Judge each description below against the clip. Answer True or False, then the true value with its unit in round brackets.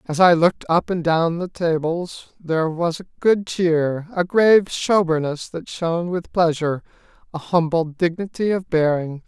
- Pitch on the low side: False (170 Hz)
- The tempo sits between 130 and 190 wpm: True (160 wpm)